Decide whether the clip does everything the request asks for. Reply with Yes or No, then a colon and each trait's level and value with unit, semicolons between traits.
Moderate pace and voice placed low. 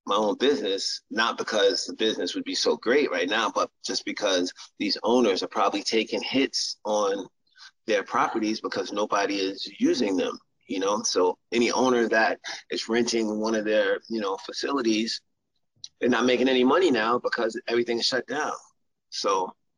Yes: average, 170 wpm; low, 120 Hz